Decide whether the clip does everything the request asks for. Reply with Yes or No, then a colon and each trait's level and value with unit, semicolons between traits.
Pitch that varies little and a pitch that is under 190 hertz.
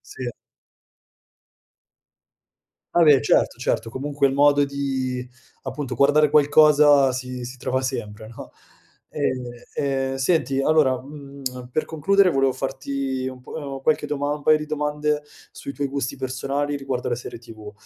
Yes: narrow, 2.3 semitones; low, 135 Hz